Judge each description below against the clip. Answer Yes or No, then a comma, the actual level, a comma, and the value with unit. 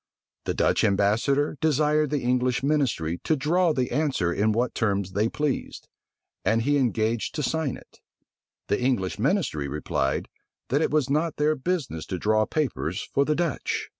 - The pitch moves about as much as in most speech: No, wide, 6.0 semitones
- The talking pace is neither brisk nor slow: Yes, average, 165 wpm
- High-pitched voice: No, low, 130 Hz